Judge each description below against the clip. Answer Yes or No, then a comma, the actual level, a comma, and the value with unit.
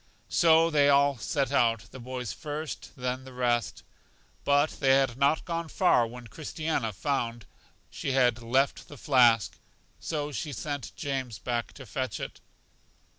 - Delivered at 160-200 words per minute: No, average, 150 wpm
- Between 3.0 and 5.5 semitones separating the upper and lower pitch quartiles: Yes, average, 3.3 semitones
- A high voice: No, low, 135 Hz